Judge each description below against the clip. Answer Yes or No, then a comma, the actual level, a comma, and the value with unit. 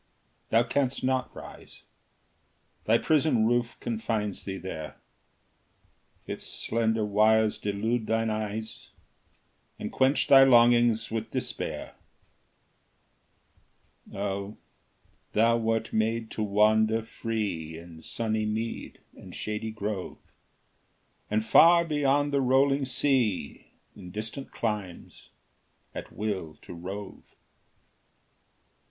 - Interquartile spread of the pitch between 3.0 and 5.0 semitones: No, narrow, 2.4 semitones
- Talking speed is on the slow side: Yes, slow, 100 wpm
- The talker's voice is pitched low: Yes, low, 110 Hz